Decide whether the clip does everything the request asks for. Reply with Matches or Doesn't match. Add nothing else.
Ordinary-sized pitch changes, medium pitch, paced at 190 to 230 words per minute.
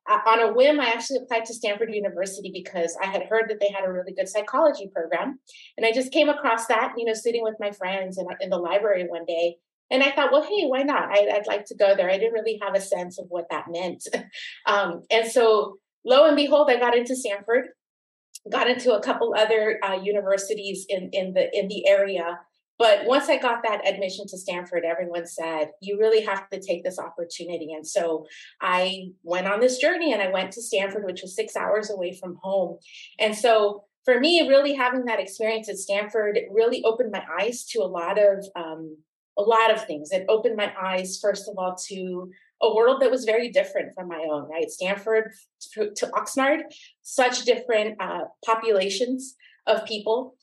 Doesn't match